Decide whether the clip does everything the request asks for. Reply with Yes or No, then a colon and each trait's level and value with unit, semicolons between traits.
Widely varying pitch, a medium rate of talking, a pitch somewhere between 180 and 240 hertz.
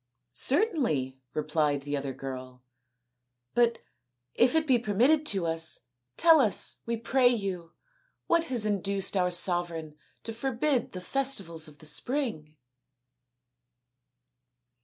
No: wide, 8.5 semitones; slow, 125 wpm; high, 190 Hz